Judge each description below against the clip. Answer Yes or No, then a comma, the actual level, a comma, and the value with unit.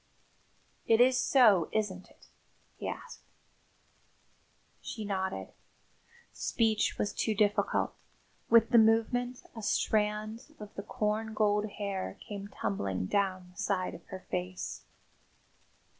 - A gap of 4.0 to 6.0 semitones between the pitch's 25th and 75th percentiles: No, average, 2.8 semitones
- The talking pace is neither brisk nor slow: No, slow, 115 wpm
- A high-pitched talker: Yes, high, 210 Hz